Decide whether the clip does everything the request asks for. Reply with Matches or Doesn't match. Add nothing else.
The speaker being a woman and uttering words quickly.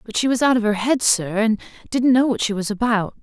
Matches